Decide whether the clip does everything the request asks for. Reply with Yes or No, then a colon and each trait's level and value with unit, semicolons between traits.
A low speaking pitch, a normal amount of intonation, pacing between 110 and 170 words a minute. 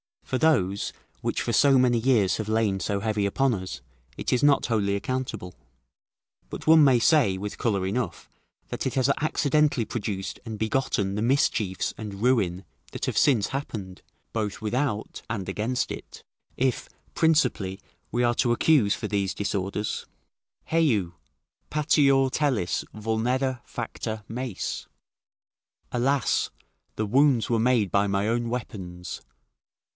Yes: low, 115 Hz; average, 4.6 semitones; average, 140 wpm